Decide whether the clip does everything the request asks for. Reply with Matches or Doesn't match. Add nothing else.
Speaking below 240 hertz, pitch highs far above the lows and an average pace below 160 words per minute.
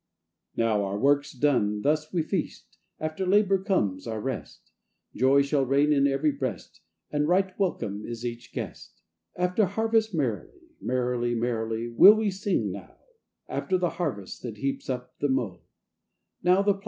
Matches